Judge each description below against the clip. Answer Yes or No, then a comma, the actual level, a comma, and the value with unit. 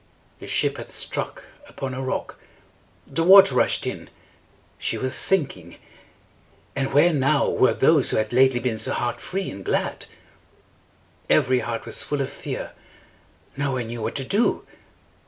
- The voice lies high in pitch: No, low, 130 Hz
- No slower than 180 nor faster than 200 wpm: No, average, 155 wpm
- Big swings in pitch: No, average, 3.4 semitones